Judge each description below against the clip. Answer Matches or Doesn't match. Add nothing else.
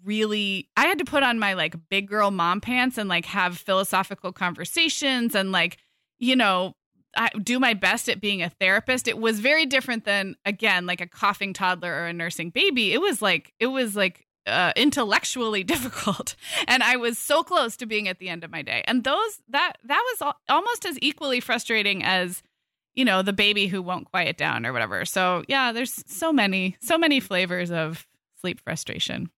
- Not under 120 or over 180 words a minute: Doesn't match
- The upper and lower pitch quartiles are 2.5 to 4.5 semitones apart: Doesn't match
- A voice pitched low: Doesn't match